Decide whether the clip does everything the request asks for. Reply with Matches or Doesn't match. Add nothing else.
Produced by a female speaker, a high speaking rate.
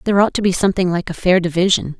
Matches